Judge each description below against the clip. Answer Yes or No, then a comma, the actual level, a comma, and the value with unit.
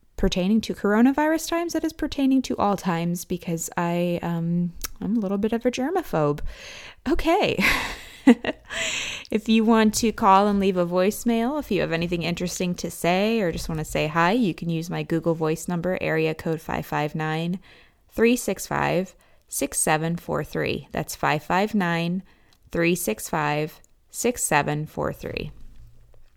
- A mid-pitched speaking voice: Yes, medium, 180 Hz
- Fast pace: No, slow, 135 wpm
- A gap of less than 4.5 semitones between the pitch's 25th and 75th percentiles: No, average, 5.3 semitones